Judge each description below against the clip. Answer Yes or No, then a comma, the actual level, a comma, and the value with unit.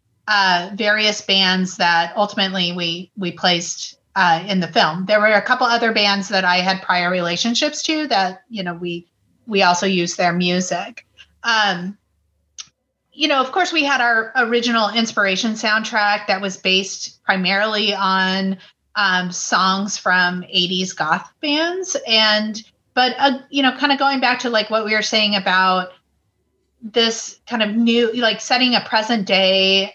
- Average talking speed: Yes, average, 160 wpm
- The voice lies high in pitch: Yes, high, 205 Hz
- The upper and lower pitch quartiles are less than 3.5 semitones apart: No, average, 3.8 semitones